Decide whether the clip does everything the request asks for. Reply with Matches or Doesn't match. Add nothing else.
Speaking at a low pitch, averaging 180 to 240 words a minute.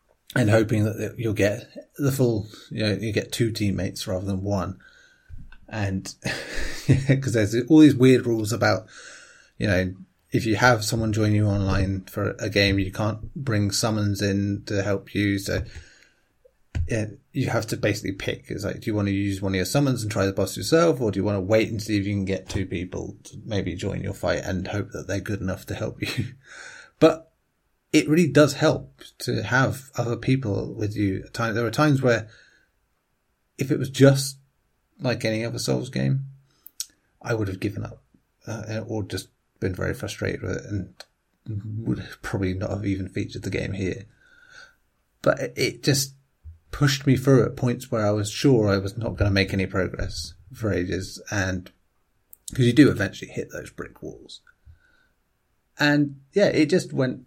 Matches